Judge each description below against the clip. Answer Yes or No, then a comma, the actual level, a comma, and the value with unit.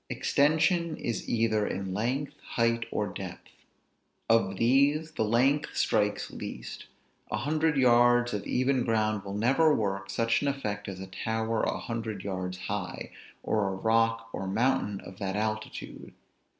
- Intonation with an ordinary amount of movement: Yes, average, 3.9 semitones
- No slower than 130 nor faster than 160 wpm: Yes, average, 150 wpm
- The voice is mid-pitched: No, low, 115 Hz